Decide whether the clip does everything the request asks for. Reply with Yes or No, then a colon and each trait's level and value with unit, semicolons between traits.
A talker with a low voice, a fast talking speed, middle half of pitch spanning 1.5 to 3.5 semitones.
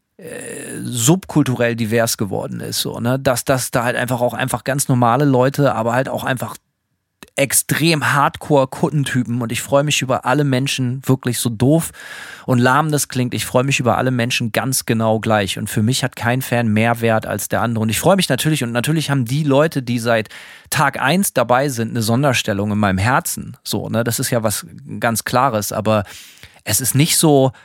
Yes: low, 125 Hz; fast, 200 wpm; average, 3.2 semitones